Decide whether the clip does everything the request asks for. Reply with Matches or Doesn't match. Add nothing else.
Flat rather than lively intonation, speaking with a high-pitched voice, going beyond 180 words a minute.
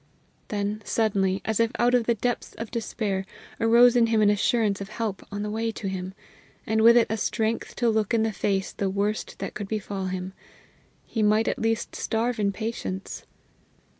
Matches